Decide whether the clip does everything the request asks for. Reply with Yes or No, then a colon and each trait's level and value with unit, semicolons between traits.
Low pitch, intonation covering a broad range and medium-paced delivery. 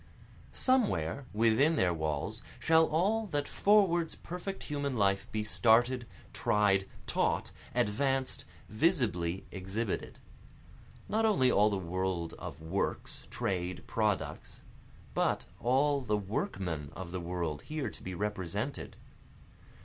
No: low, 105 Hz; wide, 7.6 semitones; slow, 115 wpm